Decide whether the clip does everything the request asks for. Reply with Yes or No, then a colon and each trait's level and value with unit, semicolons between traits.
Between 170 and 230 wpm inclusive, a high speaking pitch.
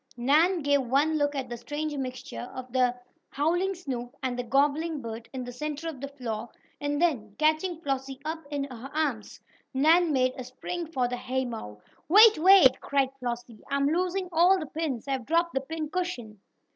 Yes: average, 185 wpm; very high, 280 Hz